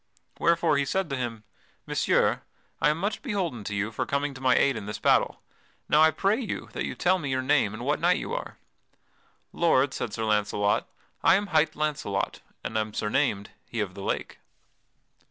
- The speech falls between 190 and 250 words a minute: Yes, average, 195 wpm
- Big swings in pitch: Yes, wide, 7.3 semitones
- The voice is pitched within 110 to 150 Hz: Yes, medium, 140 Hz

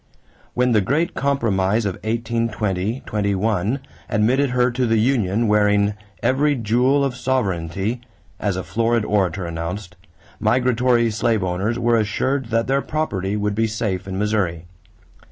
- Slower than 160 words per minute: Yes, slow, 135 wpm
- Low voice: Yes, low, 110 Hz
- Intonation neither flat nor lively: Yes, average, 3.7 semitones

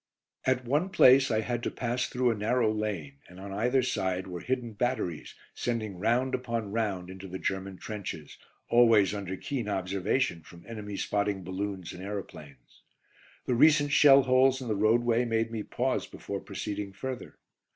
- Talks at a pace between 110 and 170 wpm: Yes, average, 165 wpm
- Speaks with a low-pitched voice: Yes, low, 110 Hz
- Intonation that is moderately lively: Yes, average, 4.4 semitones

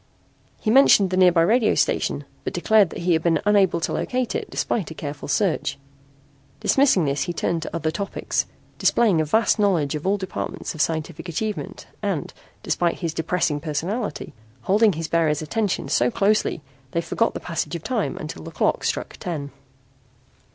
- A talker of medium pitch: Yes, medium, 175 Hz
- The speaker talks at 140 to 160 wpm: No, average, 170 wpm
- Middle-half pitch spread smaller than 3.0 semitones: No, average, 4.7 semitones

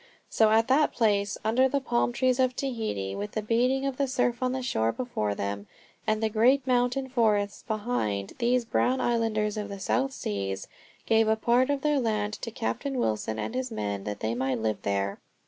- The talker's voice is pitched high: Yes, high, 225 Hz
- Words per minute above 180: Yes, average, 200 wpm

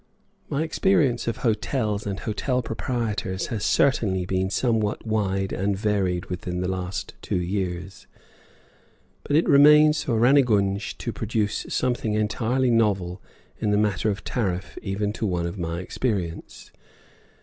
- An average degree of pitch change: Yes, average, 3.9 semitones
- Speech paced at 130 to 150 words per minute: Yes, average, 140 wpm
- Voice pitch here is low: Yes, low, 105 Hz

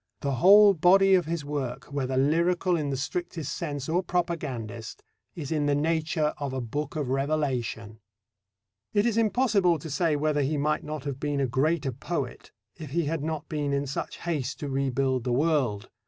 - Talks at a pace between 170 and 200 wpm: Yes, average, 185 wpm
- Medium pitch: Yes, medium, 150 Hz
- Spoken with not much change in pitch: No, average, 3.7 semitones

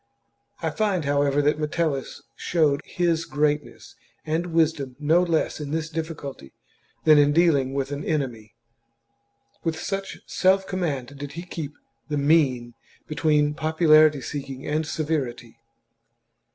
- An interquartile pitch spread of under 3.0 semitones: Yes, narrow, 2.5 semitones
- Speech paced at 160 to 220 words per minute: No, slow, 135 wpm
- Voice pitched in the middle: Yes, medium, 150 Hz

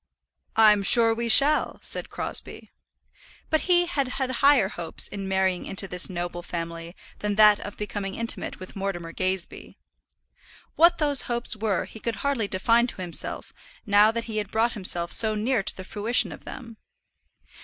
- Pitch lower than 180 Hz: No, high, 210 Hz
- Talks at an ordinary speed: Yes, average, 165 wpm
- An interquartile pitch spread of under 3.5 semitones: No, average, 3.8 semitones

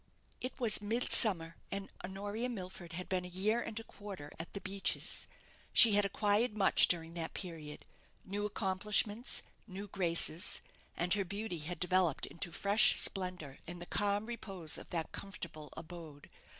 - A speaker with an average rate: Yes, average, 155 wpm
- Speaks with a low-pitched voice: No, high, 190 Hz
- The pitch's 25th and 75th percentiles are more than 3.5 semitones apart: No, average, 3.2 semitones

